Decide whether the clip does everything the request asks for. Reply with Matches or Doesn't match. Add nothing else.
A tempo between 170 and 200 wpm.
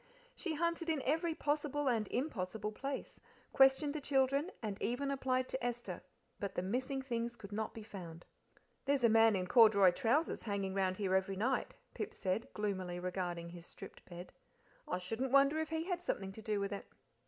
Matches